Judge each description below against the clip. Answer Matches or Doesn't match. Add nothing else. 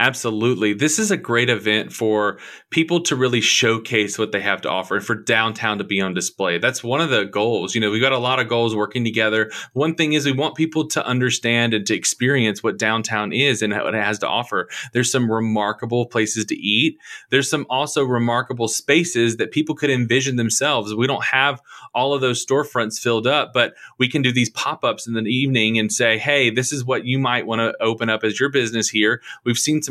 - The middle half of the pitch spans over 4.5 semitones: Doesn't match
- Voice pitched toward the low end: Matches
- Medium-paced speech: Doesn't match